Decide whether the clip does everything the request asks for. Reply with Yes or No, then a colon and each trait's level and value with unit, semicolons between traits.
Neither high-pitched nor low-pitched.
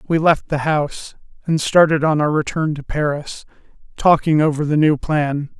Yes: medium, 150 Hz